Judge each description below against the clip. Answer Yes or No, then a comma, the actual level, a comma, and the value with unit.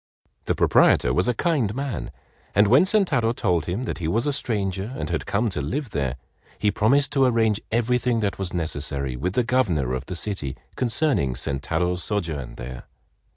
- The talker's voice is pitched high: No, low, 100 Hz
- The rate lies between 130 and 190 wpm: Yes, average, 180 wpm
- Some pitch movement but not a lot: No, wide, 8.1 semitones